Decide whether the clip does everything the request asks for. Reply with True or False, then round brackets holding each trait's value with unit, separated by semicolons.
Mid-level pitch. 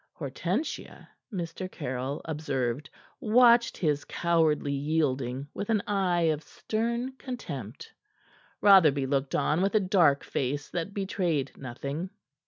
True (160 Hz)